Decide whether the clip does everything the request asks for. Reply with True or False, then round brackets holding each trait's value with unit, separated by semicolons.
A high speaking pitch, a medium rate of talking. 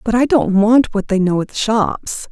False (220 Hz; 235 wpm)